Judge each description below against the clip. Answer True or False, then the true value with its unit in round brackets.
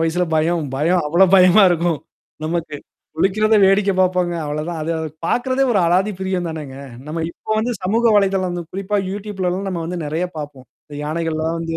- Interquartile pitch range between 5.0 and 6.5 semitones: False (3.1 semitones)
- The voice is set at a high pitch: False (175 Hz)